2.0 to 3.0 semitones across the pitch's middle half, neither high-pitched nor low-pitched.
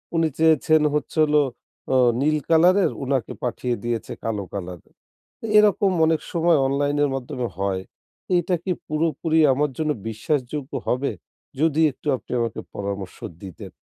No: average, 5.3 semitones; medium, 145 Hz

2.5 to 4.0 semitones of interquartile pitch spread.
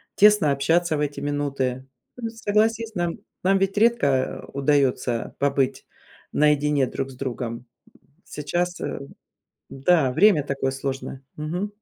No: average, 4.8 semitones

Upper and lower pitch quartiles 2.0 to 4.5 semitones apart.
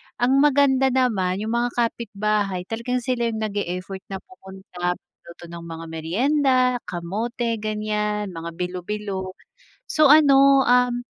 No: average, 5.2 semitones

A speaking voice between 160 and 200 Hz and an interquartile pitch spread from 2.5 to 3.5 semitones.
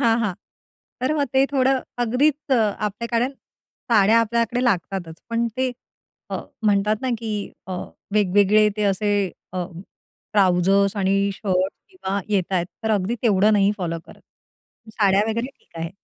No: high, 210 Hz; average, 3.2 semitones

